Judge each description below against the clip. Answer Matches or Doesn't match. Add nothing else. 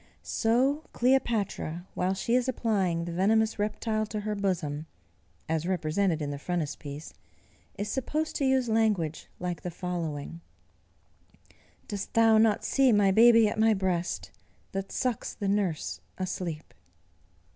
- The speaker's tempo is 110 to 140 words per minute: Matches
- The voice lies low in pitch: Doesn't match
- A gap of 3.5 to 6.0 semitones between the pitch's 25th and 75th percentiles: Matches